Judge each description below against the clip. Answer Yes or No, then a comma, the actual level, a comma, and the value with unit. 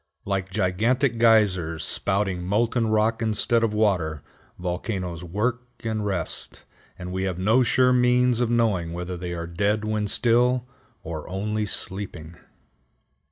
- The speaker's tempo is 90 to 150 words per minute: Yes, slow, 135 wpm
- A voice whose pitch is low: Yes, low, 105 Hz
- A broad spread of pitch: No, average, 4.2 semitones